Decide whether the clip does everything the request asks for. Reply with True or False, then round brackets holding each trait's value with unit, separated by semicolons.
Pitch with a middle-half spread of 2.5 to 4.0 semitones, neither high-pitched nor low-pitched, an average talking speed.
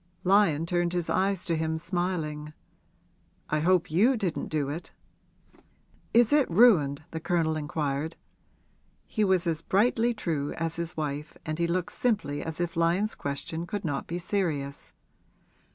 True (3.5 semitones; 170 Hz; 150 wpm)